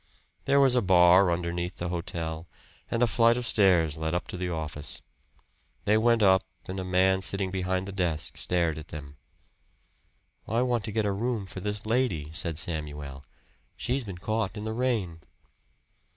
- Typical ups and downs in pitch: Yes, average, 4.6 semitones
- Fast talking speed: No, average, 175 wpm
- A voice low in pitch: Yes, very low, 95 Hz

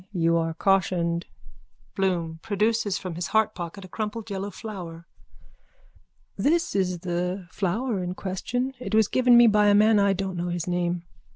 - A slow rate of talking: No, average, 160 wpm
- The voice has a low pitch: No, high, 190 Hz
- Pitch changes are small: No, average, 3.6 semitones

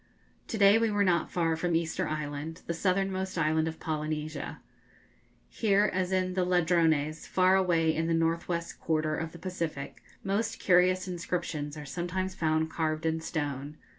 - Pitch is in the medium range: Yes, medium, 165 Hz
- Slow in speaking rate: No, average, 165 wpm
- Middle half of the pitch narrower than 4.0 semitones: Yes, average, 2.7 semitones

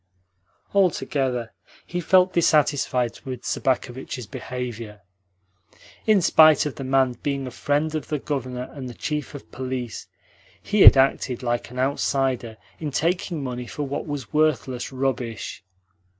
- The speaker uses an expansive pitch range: No, average, 3.2 semitones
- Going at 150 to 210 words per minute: No, slow, 135 wpm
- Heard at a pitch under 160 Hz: Yes, low, 135 Hz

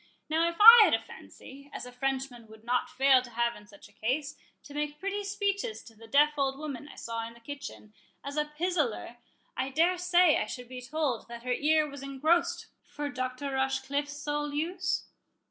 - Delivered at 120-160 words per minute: No, average, 200 wpm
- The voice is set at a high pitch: Yes, very high, 280 Hz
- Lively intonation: No, average, 3.7 semitones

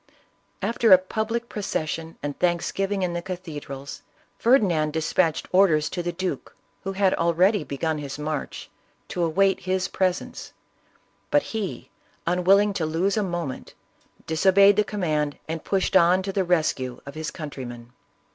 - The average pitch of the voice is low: No, medium, 175 Hz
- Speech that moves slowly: No, average, 145 wpm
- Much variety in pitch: No, average, 3.8 semitones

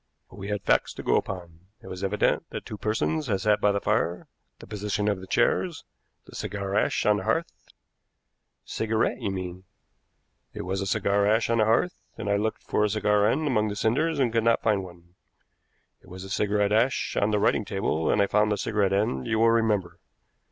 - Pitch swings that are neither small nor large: No, narrow, 2.2 semitones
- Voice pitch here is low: Yes, low, 105 Hz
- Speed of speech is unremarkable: No, fast, 215 wpm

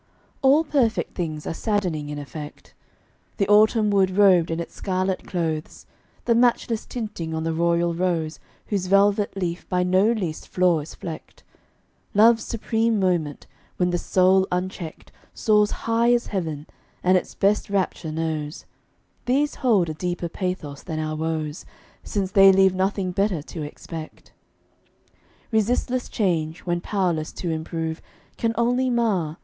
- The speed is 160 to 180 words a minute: No, average, 145 wpm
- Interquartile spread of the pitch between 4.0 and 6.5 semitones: Yes, average, 4.3 semitones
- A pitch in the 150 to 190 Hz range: Yes, medium, 185 Hz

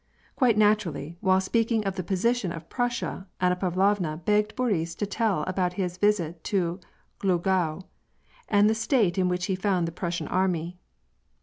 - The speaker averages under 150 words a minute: No, average, 160 wpm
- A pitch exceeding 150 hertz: Yes, medium, 185 Hz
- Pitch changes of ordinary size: Yes, average, 3.2 semitones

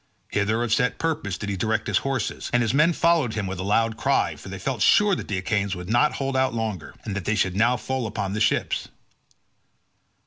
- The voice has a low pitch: Yes, low, 110 Hz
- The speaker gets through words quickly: Yes, fast, 230 wpm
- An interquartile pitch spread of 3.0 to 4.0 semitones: No, average, 4.6 semitones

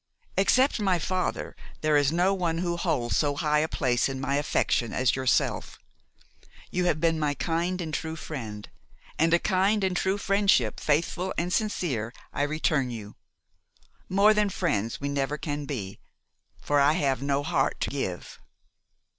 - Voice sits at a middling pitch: Yes, medium, 155 Hz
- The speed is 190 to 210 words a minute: No, average, 165 wpm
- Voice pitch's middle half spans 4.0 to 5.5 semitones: Yes, average, 4.7 semitones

